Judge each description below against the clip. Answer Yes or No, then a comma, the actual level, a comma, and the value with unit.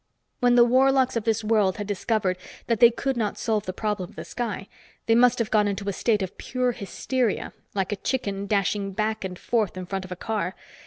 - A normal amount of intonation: Yes, average, 3.2 semitones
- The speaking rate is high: Yes, fast, 220 wpm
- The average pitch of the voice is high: Yes, high, 215 Hz